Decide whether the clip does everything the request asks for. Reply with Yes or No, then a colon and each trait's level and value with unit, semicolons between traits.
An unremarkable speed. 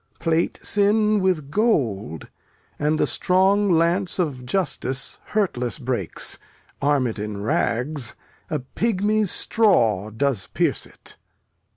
No: slow, 110 wpm